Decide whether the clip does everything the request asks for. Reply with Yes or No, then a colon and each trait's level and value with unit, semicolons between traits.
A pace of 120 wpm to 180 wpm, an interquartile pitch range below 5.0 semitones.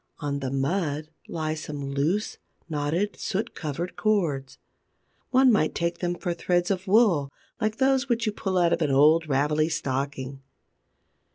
No: average, 155 wpm; wide, 5.4 semitones